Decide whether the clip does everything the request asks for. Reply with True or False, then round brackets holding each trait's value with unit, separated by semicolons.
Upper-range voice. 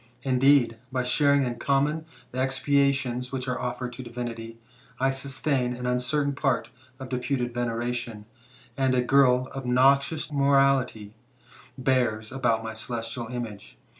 False (125 Hz)